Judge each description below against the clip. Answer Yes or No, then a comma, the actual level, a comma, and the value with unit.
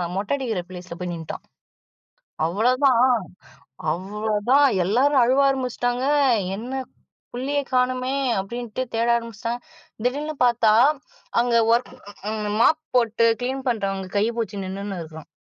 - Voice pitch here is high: Yes, high, 235 Hz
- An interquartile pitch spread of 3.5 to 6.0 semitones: Yes, average, 4.0 semitones